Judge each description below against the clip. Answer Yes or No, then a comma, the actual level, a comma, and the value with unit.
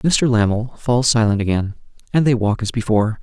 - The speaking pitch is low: Yes, low, 115 Hz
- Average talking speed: Yes, average, 185 wpm